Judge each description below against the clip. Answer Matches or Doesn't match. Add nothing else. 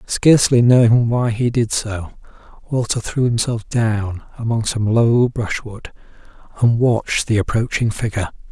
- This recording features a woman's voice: Doesn't match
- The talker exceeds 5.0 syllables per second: Doesn't match